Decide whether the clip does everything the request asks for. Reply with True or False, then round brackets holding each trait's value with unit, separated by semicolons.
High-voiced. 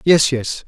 False (140 Hz)